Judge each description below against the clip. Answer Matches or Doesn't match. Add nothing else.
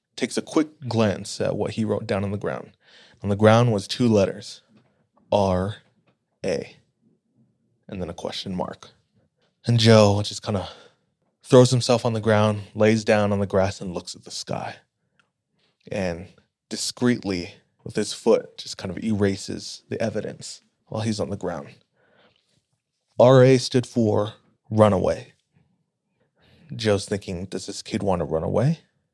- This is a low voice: Matches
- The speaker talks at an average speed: Matches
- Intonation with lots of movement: Doesn't match